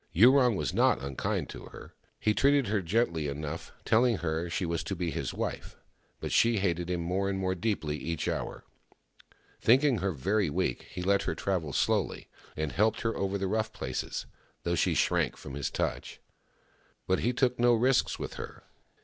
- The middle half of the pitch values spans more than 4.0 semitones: Yes, average, 5.1 semitones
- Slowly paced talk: No, average, 185 wpm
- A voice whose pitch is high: No, very low, 95 Hz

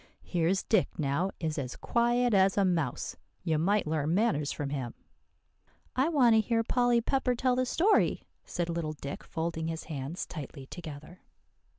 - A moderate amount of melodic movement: No, wide, 7.4 semitones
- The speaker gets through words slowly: No, average, 165 wpm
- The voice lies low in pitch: No, medium, 175 Hz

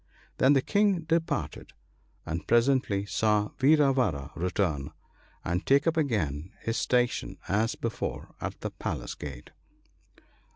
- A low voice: Yes, low, 115 Hz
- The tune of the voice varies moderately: No, wide, 7.9 semitones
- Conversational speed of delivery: No, slow, 125 wpm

